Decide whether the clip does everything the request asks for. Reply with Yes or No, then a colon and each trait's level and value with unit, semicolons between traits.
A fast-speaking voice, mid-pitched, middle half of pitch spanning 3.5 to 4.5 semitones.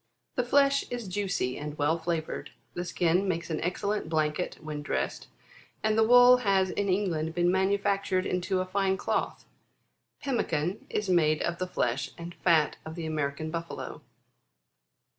No: average, 160 wpm; medium, 180 Hz; average, 4.0 semitones